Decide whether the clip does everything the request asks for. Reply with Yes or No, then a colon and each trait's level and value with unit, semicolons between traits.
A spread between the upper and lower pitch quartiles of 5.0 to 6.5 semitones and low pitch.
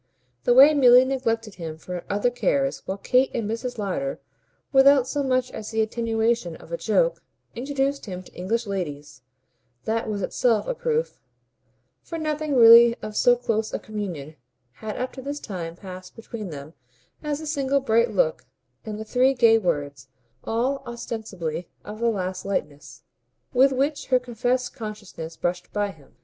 No: average, 5.3 semitones; high, 230 Hz